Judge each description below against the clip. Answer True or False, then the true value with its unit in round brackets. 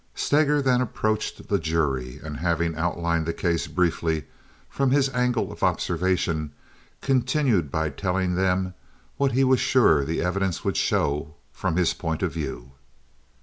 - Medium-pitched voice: False (90 Hz)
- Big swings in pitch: True (7.2 semitones)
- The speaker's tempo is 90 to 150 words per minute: True (145 wpm)